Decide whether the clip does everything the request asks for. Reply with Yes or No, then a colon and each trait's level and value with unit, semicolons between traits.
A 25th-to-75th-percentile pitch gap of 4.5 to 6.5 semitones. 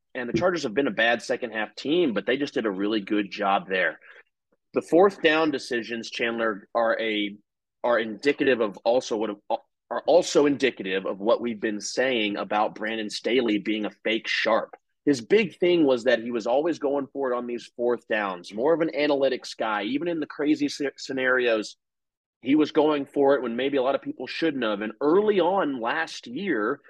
Yes: average, 5.1 semitones